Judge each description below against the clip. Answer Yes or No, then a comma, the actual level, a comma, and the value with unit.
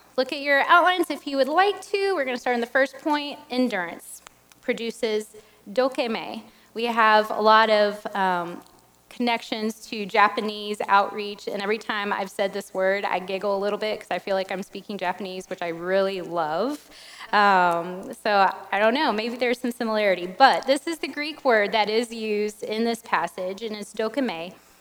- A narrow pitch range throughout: No, average, 4.1 semitones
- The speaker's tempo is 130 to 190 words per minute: Yes, average, 185 wpm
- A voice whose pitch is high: Yes, high, 215 Hz